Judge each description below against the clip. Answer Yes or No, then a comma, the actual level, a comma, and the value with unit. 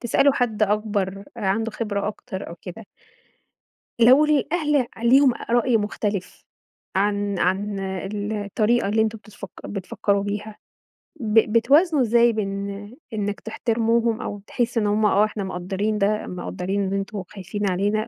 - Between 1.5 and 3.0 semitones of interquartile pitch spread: Yes, narrow, 2.5 semitones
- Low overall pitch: No, high, 210 Hz